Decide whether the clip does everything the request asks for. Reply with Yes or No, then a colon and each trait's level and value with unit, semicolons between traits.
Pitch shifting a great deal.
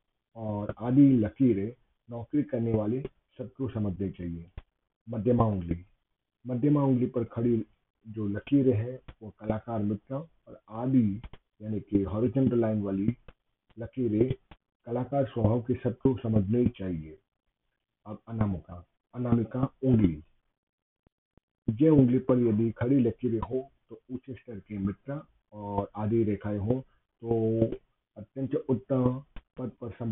No: average, 3.2 semitones